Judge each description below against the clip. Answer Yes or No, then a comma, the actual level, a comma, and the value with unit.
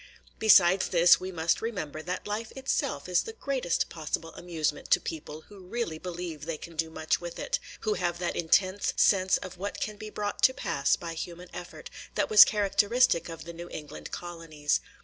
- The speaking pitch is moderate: Yes, medium, 175 Hz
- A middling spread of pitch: Yes, average, 3.8 semitones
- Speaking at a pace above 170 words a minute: Yes, average, 190 wpm